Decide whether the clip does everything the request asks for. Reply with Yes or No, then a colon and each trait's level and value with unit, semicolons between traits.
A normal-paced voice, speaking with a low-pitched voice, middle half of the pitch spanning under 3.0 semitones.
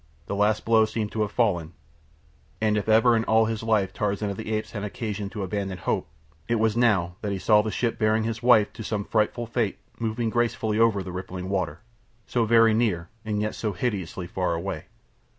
No: fast, 210 wpm; low, 105 Hz; narrow, 2.4 semitones